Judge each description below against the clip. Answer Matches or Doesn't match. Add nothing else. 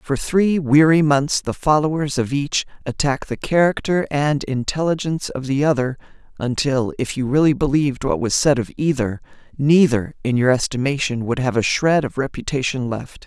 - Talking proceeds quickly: Doesn't match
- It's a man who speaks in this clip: Doesn't match